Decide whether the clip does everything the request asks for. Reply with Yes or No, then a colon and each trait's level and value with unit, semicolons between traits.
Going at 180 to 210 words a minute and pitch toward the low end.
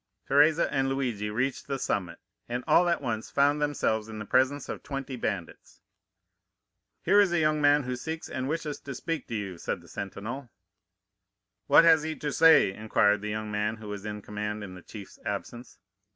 Yes: average, 190 wpm; low, 125 Hz